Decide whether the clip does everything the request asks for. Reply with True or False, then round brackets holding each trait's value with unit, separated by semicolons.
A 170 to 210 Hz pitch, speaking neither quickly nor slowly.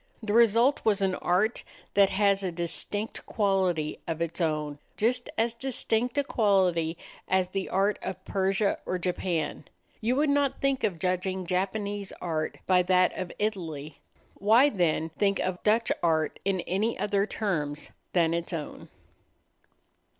True (190 Hz; 150 wpm)